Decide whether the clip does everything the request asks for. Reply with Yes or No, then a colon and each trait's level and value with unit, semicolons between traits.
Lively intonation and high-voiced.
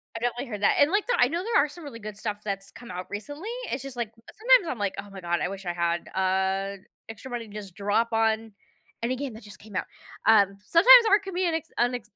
Yes: wide, 6.3 semitones; high, 225 Hz